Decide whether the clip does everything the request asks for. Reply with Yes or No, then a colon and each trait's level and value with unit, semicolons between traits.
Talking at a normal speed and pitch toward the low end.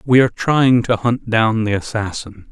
Yes: average, 190 wpm; low, 110 Hz